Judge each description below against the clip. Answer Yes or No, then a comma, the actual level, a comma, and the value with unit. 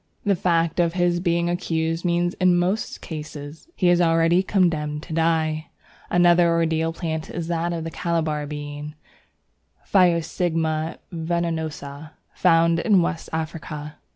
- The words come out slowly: Yes, slow, 125 wpm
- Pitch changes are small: Yes, narrow, 1.6 semitones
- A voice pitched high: No, medium, 165 Hz